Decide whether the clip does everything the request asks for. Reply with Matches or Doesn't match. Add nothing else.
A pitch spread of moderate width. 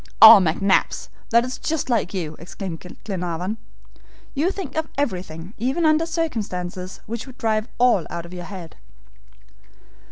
Doesn't match